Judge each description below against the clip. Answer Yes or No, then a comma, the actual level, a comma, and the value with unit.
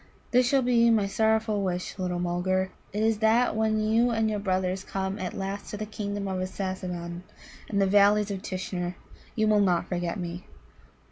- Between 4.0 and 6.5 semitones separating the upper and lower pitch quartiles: No, average, 2.7 semitones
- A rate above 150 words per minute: Yes, average, 185 wpm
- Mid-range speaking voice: No, high, 200 Hz